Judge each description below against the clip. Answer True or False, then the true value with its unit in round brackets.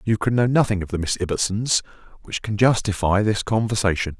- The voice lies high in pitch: False (105 Hz)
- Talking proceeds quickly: False (185 wpm)